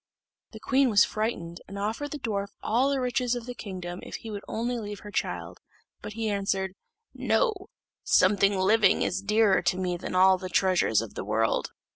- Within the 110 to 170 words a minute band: No, average, 195 wpm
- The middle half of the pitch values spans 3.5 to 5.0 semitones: Yes, average, 3.8 semitones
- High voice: Yes, high, 205 Hz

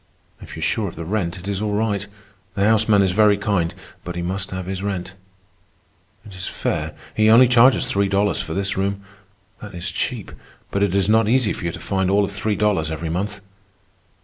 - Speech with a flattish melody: Yes, narrow, 2.1 semitones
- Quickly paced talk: Yes, fast, 215 wpm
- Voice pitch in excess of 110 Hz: No, low, 100 Hz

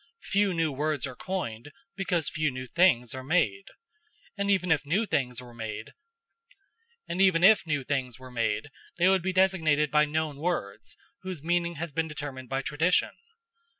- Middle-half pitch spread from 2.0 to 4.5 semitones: No, wide, 5.5 semitones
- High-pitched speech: No, medium, 150 Hz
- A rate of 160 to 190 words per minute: No, average, 140 wpm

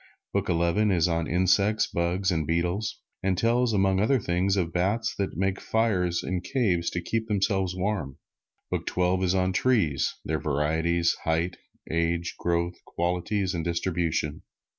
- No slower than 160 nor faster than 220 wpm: No, average, 150 wpm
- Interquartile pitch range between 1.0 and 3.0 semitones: Yes, narrow, 2.6 semitones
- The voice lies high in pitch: No, very low, 90 Hz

